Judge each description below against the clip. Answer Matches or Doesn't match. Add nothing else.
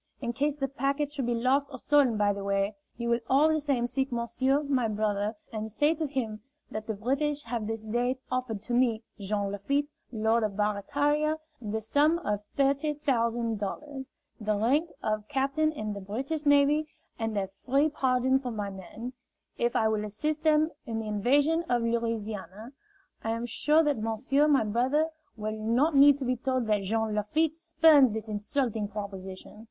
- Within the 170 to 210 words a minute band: Matches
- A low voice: Doesn't match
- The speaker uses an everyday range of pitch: Matches